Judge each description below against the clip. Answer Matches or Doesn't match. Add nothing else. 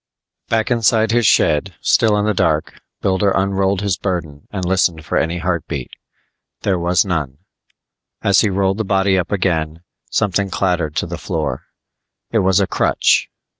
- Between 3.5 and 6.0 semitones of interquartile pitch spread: Doesn't match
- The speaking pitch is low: Matches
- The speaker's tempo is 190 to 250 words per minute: Doesn't match